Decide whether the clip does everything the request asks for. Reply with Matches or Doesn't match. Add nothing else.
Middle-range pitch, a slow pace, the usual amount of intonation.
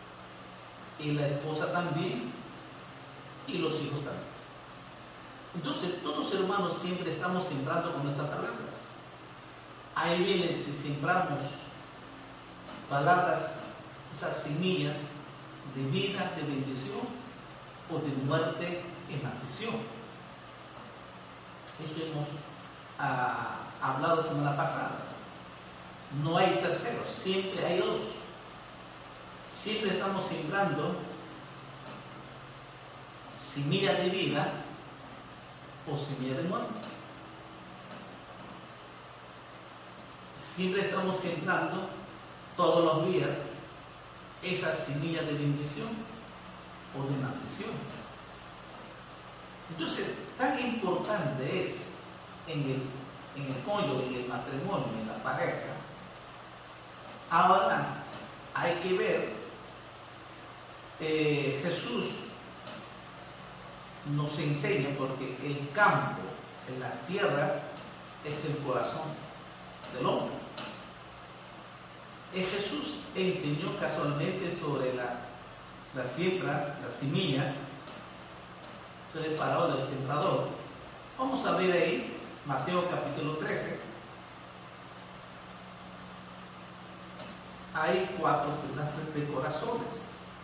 Matches